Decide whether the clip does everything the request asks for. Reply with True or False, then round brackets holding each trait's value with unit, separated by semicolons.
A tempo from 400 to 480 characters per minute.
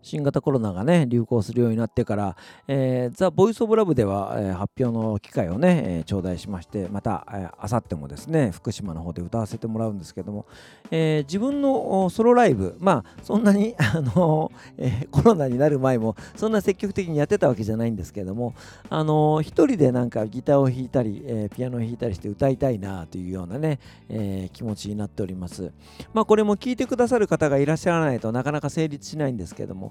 True (440 characters per minute)